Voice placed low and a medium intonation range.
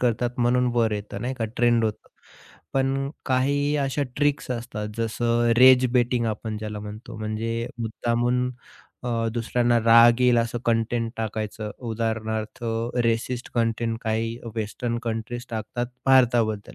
No: low, 115 Hz; narrow, 1.6 semitones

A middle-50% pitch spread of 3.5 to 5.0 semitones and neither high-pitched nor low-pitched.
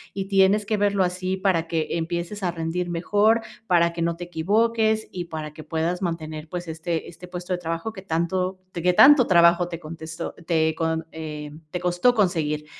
No: average, 2.7 semitones; medium, 175 Hz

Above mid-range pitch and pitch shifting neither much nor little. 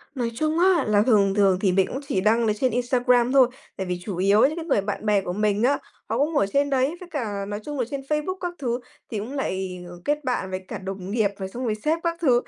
No: high, 235 Hz; wide, 5.9 semitones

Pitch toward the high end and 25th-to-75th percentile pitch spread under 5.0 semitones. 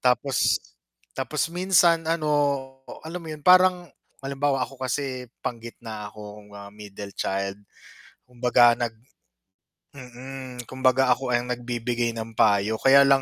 No: low, 125 Hz; average, 3.3 semitones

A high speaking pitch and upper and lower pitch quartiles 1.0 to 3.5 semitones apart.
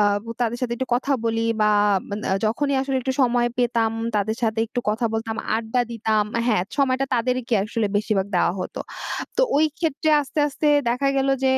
Yes: high, 240 Hz; average, 3.1 semitones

